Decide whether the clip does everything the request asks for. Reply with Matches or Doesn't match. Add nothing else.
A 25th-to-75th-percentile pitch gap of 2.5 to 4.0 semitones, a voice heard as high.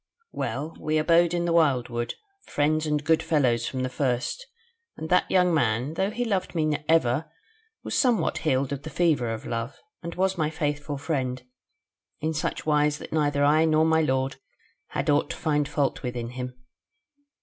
Doesn't match